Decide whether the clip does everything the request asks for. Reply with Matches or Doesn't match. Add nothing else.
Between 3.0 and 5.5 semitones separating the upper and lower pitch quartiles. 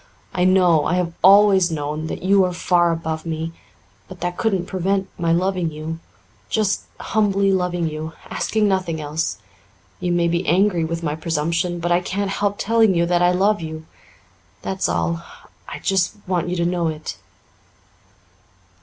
Doesn't match